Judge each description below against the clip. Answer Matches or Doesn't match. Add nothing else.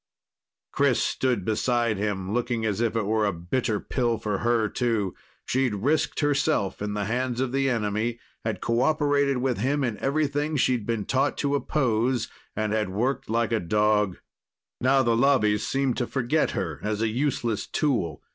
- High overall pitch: Doesn't match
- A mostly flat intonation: Doesn't match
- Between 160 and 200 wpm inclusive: Matches